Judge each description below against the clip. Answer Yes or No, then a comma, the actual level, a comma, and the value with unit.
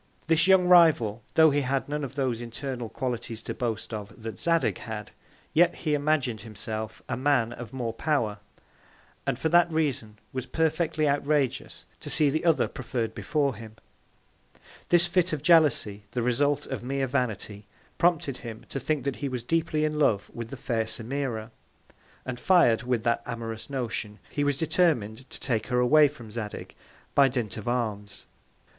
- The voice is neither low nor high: No, low, 130 Hz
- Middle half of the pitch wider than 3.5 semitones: Yes, average, 5.0 semitones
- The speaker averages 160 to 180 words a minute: Yes, average, 170 wpm